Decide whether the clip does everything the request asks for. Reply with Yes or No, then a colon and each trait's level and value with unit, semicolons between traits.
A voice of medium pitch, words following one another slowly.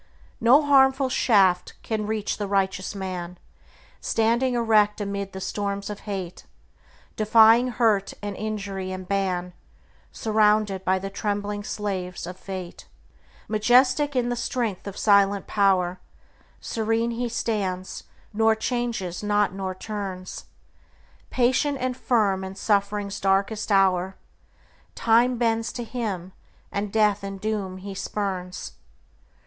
No: high, 205 Hz; slow, 120 wpm